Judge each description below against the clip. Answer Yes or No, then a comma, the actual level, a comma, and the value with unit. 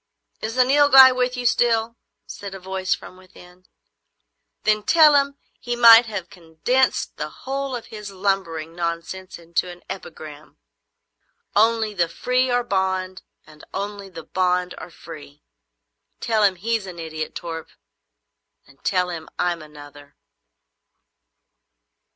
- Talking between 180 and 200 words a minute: No, slow, 135 wpm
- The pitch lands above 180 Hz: Yes, high, 190 Hz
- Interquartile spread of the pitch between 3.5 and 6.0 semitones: Yes, wide, 5.5 semitones